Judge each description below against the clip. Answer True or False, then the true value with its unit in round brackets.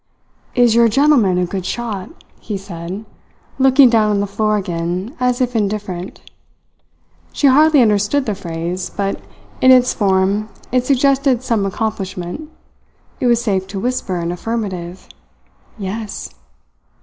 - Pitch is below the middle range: False (210 Hz)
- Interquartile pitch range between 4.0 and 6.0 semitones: True (4.6 semitones)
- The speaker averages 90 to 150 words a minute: True (135 wpm)